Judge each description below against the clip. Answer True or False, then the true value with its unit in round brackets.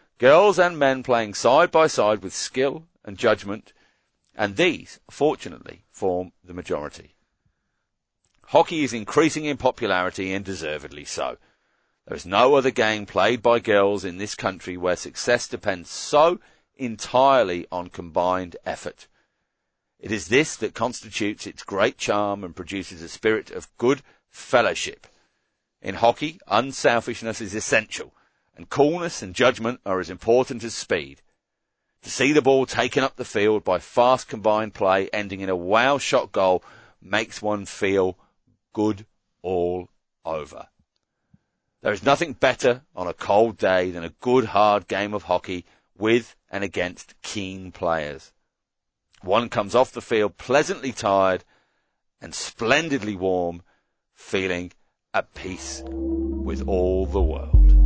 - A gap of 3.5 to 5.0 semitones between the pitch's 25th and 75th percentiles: True (4.7 semitones)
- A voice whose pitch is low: True (100 Hz)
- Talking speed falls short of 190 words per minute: True (140 wpm)